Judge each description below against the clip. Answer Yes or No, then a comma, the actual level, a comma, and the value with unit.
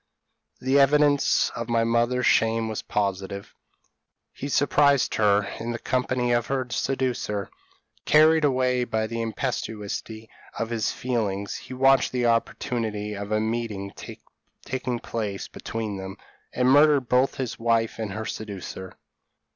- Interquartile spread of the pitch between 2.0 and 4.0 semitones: Yes, average, 3.1 semitones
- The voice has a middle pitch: No, low, 115 Hz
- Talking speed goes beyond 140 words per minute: No, slow, 135 wpm